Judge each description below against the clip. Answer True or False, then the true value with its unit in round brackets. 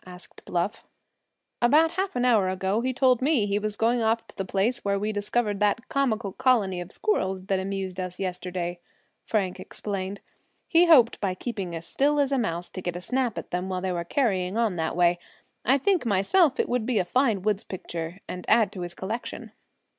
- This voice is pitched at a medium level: False (205 Hz)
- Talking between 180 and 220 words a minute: True (205 wpm)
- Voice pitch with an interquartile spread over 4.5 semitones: True (4.9 semitones)